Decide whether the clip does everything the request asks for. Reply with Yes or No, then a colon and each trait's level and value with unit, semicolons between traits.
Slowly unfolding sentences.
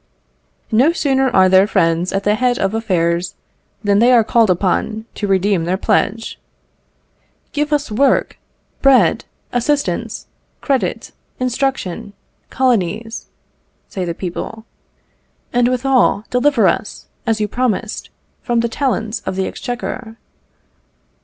Yes: slow, 120 wpm